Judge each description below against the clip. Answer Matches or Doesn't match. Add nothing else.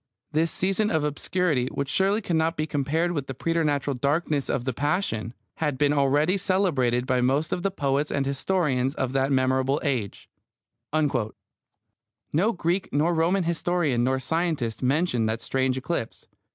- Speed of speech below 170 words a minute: Matches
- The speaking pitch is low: Doesn't match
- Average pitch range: Matches